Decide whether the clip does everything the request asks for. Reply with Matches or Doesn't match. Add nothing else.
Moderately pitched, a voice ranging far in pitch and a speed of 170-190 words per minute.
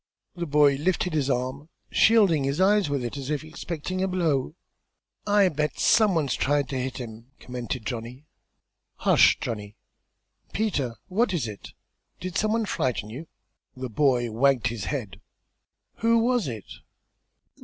Doesn't match